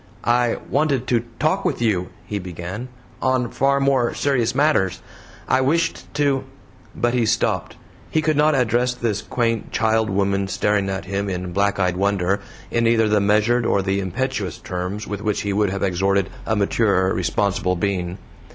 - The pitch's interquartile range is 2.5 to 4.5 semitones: Yes, average, 4.1 semitones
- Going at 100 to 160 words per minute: No, average, 170 wpm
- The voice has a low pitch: Yes, low, 105 Hz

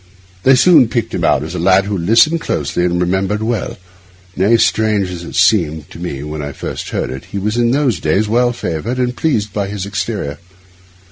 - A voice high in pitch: No, low, 100 Hz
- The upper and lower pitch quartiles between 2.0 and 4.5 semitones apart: No, average, 5.0 semitones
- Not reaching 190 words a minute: No, fast, 205 wpm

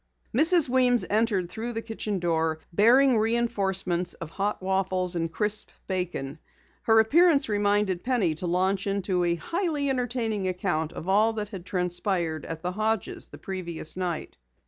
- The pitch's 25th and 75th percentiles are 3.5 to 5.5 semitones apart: Yes, average, 4.1 semitones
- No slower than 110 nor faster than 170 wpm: Yes, average, 150 wpm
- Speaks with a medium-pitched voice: No, high, 195 Hz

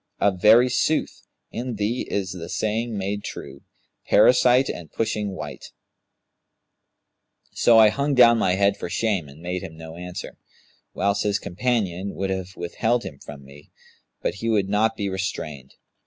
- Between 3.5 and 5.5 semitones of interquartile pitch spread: Yes, average, 4.1 semitones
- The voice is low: Yes, low, 100 Hz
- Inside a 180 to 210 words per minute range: No, average, 155 wpm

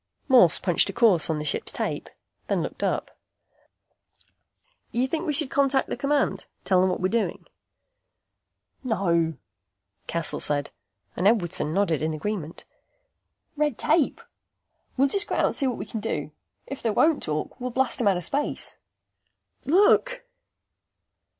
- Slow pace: No, average, 150 wpm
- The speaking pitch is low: No, high, 225 Hz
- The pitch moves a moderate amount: No, wide, 8.4 semitones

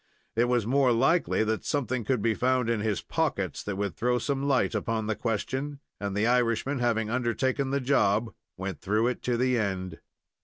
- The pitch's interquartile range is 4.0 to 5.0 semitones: No, average, 3.2 semitones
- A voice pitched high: No, low, 120 Hz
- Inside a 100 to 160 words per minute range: No, average, 190 wpm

